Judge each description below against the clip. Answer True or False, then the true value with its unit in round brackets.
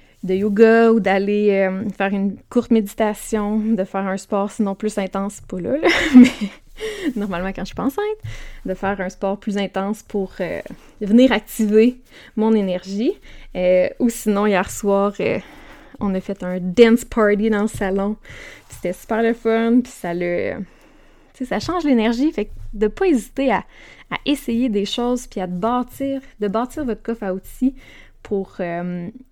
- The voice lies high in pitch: True (215 Hz)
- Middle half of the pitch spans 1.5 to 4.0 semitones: True (3.7 semitones)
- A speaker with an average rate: True (175 wpm)